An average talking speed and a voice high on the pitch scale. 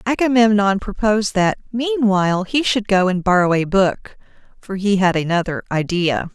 Yes: average, 150 wpm; high, 200 Hz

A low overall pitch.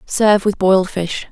No: high, 195 Hz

